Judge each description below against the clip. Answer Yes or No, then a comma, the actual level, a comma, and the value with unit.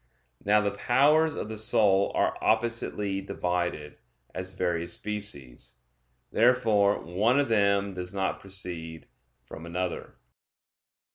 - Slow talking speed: Yes, slow, 115 wpm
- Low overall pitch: Yes, low, 100 Hz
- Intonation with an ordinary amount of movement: Yes, average, 3.6 semitones